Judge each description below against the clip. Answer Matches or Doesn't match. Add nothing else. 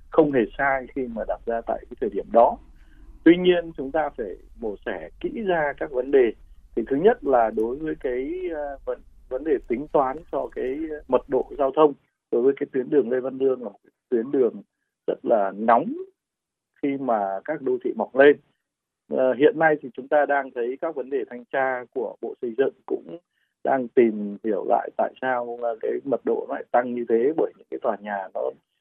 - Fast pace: Doesn't match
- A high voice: Doesn't match